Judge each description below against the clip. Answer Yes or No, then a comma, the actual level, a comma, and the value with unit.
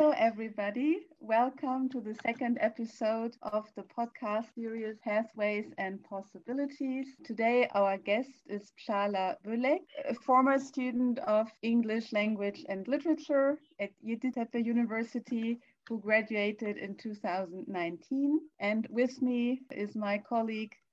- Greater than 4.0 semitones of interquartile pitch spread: No, average, 3.5 semitones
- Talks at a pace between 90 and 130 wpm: Yes, average, 120 wpm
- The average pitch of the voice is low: No, high, 230 Hz